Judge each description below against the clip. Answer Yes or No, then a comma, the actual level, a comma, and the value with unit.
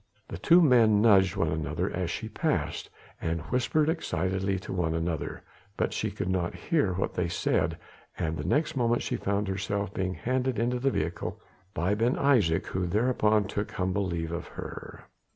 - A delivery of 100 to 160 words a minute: No, average, 175 wpm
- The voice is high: No, low, 100 Hz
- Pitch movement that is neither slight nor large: No, wide, 5.8 semitones